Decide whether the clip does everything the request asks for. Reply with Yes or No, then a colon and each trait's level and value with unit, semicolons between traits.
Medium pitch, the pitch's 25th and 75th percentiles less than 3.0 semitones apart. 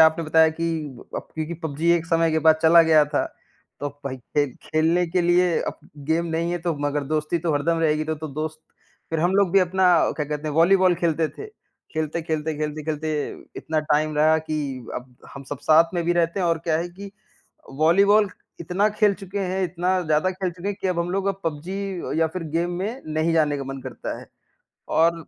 Yes: medium, 165 Hz; narrow, 2.4 semitones